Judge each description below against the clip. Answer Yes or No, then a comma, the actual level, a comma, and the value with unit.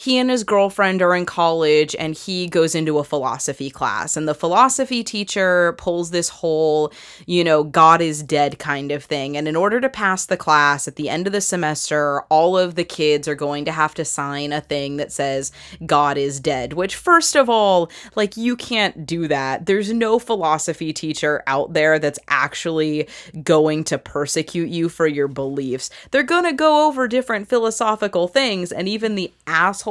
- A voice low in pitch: No, medium, 165 Hz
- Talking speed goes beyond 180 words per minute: Yes, average, 190 wpm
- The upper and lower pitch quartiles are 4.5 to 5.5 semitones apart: Yes, average, 5.0 semitones